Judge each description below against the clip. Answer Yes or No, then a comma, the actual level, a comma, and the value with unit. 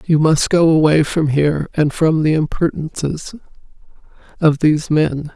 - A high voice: No, medium, 155 Hz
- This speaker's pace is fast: No, average, 145 wpm